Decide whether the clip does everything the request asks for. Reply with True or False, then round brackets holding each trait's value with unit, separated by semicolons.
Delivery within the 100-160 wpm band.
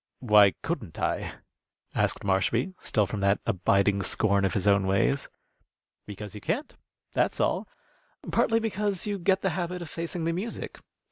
True (155 wpm)